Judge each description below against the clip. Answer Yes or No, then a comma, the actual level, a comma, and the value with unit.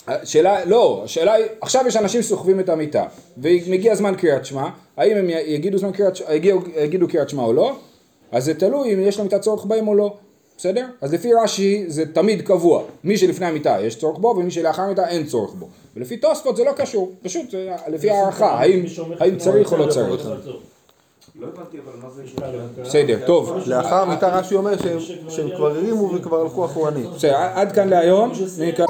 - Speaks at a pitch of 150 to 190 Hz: Yes, medium, 185 Hz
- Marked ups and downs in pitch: No, average, 4.0 semitones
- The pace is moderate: No, fast, 165 wpm